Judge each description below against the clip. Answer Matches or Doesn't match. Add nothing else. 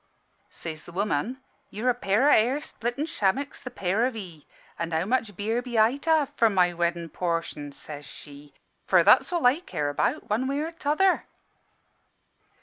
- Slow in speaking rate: Doesn't match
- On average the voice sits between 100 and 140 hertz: Doesn't match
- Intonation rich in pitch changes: Matches